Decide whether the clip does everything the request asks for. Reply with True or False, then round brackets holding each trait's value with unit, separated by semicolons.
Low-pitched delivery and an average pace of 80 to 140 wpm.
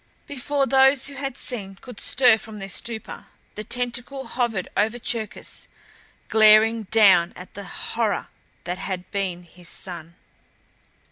False (220 Hz; 135 wpm)